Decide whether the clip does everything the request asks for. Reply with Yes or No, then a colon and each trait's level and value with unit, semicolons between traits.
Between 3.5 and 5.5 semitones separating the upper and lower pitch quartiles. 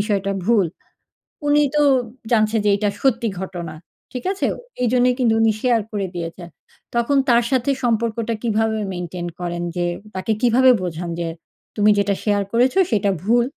Yes: average, 3.9 semitones